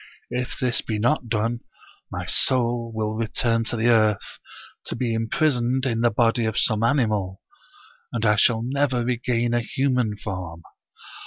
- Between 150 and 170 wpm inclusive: Yes, average, 155 wpm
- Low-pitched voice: Yes, low, 115 Hz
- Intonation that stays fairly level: Yes, narrow, 2.1 semitones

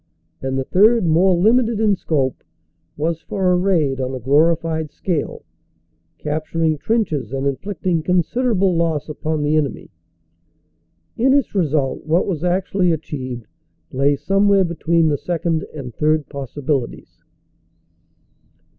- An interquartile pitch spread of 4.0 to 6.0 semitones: Yes, average, 4.3 semitones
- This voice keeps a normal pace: No, slow, 130 wpm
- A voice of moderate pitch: Yes, medium, 160 Hz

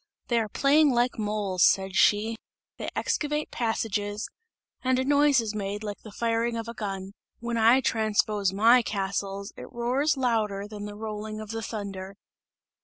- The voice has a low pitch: No, high, 220 Hz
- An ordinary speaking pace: Yes, average, 165 wpm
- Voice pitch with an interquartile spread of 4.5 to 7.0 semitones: No, narrow, 2.6 semitones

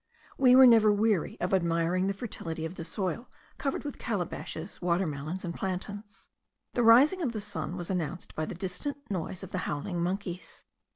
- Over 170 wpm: Yes, average, 180 wpm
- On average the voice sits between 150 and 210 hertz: Yes, medium, 185 Hz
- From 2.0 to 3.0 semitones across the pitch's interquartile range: No, average, 4.1 semitones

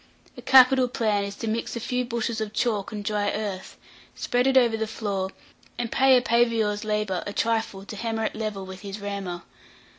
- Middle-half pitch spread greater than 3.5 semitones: No, narrow, 2.5 semitones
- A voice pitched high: Yes, high, 220 Hz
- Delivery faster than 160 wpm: Yes, average, 200 wpm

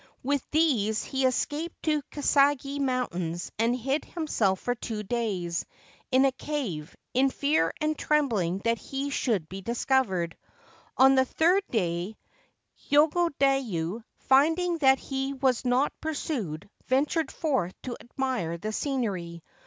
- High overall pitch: Yes, very high, 260 Hz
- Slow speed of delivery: Yes, slow, 130 wpm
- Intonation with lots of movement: Yes, wide, 5.9 semitones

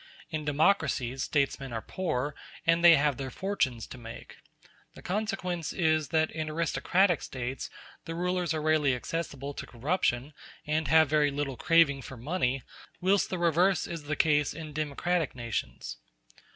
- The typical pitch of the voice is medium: Yes, medium, 155 Hz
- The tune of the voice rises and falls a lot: No, average, 3.8 semitones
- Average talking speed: Yes, average, 150 wpm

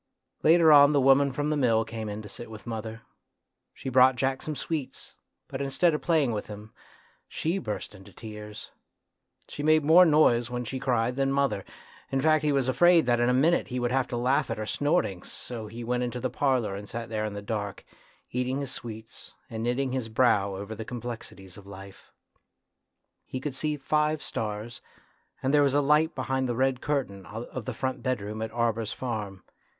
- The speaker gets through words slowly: No, average, 200 wpm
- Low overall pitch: Yes, low, 125 Hz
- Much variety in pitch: No, average, 4.0 semitones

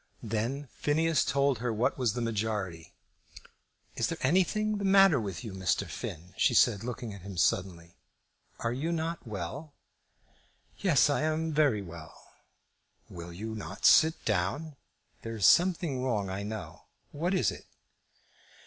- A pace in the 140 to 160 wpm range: Yes, average, 150 wpm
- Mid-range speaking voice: No, low, 115 Hz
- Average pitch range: No, wide, 7.6 semitones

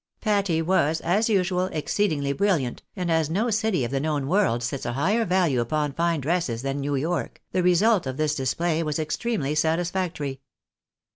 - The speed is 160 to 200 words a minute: Yes, average, 170 wpm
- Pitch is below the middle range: No, medium, 160 Hz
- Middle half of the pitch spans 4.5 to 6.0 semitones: Yes, average, 4.8 semitones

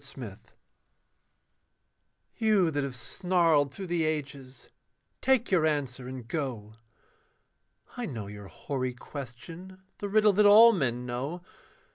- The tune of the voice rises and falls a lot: Yes, wide, 6.6 semitones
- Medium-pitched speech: Yes, medium, 150 Hz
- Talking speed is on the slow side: Yes, slow, 125 wpm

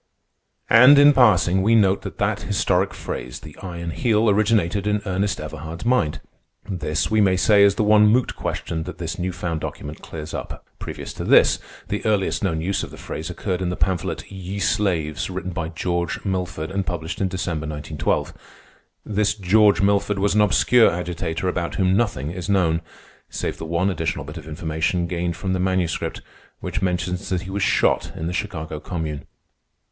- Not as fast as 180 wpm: No, average, 185 wpm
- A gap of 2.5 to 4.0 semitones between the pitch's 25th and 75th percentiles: Yes, average, 3.5 semitones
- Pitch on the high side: No, very low, 90 Hz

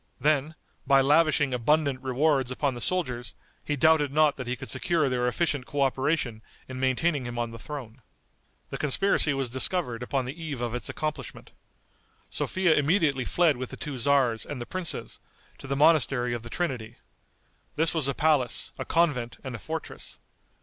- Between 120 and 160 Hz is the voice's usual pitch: Yes, low, 135 Hz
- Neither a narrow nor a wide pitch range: Yes, average, 3.8 semitones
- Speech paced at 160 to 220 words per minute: Yes, average, 170 wpm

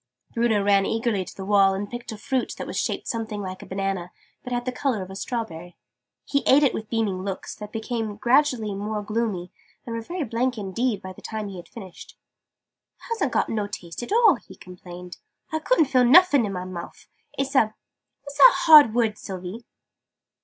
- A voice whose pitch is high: Yes, high, 220 Hz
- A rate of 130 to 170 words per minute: No, fast, 205 wpm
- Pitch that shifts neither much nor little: Yes, average, 4.3 semitones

